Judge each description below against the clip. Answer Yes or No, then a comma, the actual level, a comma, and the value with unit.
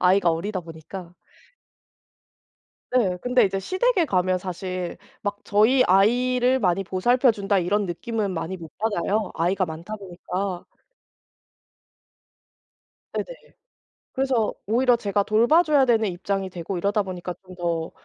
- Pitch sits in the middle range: No, high, 195 Hz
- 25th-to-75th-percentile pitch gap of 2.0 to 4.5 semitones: Yes, average, 4.2 semitones